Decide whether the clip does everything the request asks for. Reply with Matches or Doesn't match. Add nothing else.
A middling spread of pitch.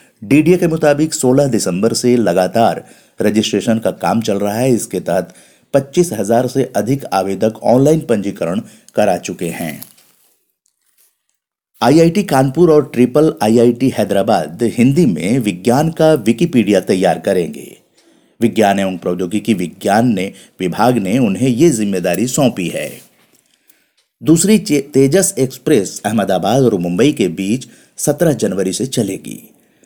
Doesn't match